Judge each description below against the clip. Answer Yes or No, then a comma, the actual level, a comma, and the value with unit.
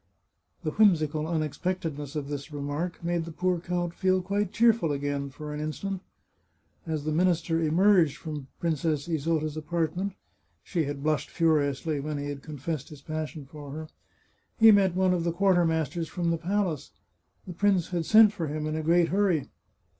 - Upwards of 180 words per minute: No, average, 170 wpm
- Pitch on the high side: No, medium, 160 Hz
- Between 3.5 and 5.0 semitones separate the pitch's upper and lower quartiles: No, average, 2.9 semitones